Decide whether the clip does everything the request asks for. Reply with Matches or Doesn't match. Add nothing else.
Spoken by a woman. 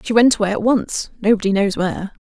Matches